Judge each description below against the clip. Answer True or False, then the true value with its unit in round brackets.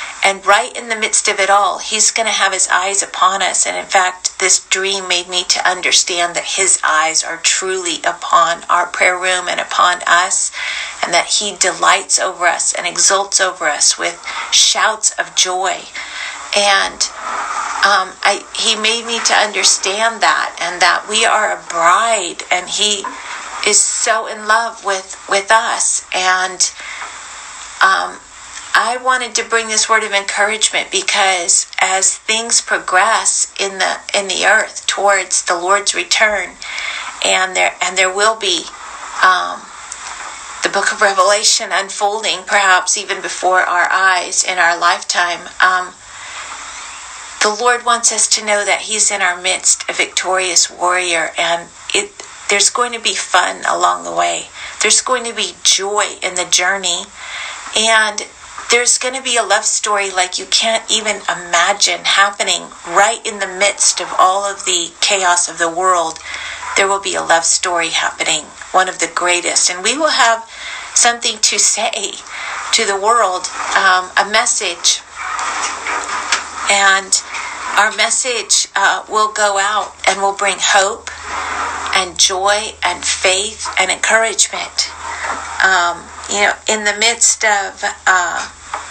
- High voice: True (200 Hz)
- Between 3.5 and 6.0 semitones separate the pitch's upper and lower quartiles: False (3.1 semitones)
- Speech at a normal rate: True (150 wpm)